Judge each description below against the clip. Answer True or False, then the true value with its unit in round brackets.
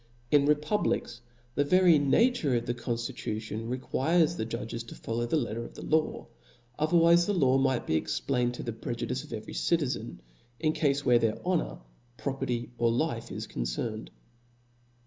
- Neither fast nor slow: True (160 wpm)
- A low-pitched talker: True (130 Hz)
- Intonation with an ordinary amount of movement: True (4.7 semitones)